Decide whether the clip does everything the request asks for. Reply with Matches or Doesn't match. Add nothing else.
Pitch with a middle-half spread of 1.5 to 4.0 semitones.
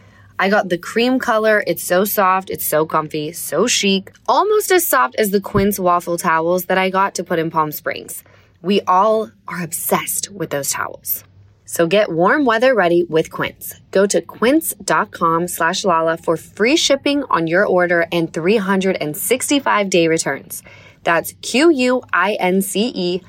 Doesn't match